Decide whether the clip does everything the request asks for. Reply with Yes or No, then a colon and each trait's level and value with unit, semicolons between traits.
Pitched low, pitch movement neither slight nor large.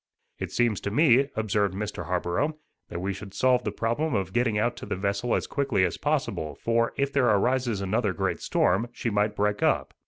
Yes: low, 110 Hz; average, 3.8 semitones